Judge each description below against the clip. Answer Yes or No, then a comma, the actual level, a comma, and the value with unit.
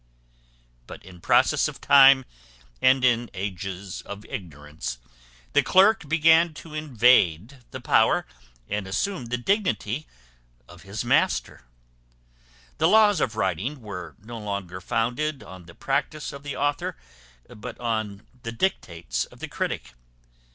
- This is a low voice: Yes, low, 115 Hz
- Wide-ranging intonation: Yes, wide, 6.8 semitones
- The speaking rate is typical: No, slow, 130 wpm